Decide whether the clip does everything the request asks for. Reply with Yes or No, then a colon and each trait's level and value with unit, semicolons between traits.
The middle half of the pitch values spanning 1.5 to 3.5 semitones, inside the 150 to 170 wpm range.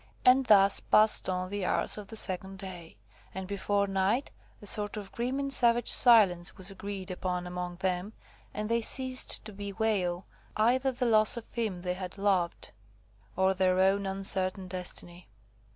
Yes: average, 3.0 semitones; average, 165 wpm